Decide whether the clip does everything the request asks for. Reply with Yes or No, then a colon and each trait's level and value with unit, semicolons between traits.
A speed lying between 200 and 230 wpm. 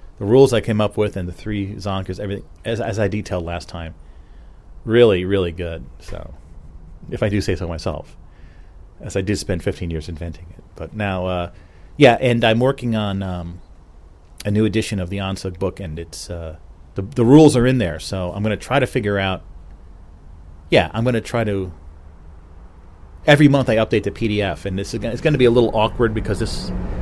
Yes: fast, 205 wpm